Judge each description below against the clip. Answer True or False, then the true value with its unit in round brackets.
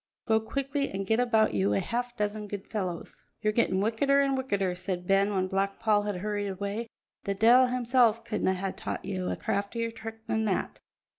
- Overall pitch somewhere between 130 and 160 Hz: False (210 Hz)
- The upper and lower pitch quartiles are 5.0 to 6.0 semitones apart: False (3.0 semitones)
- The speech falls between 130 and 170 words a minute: False (195 wpm)